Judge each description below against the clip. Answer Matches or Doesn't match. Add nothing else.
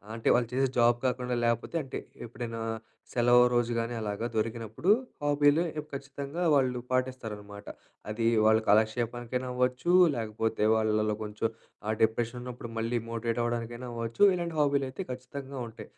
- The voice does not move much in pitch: Matches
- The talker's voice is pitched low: Matches